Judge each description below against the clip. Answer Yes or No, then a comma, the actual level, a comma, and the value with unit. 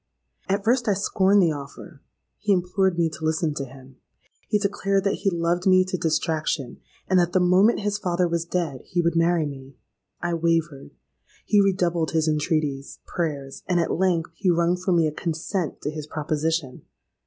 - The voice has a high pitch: No, medium, 170 Hz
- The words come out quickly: No, average, 175 wpm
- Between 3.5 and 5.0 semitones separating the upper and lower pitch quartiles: No, average, 3.1 semitones